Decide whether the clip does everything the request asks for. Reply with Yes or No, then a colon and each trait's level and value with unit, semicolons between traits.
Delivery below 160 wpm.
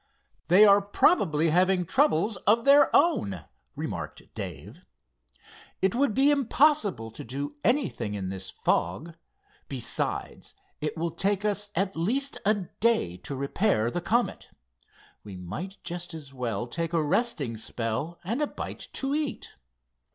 Yes: average, 140 wpm